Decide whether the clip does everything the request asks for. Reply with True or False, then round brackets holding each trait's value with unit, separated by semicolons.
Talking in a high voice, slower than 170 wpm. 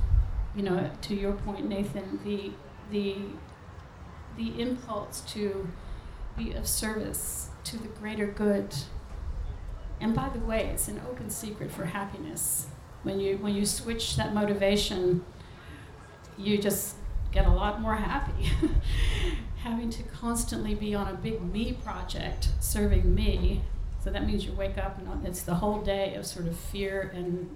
True (195 Hz; 150 wpm)